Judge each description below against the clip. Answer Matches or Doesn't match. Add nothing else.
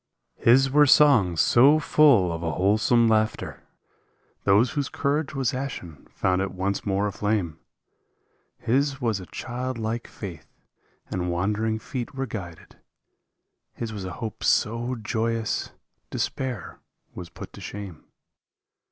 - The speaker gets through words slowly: Matches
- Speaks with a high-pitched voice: Doesn't match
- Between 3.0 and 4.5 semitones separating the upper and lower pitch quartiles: Doesn't match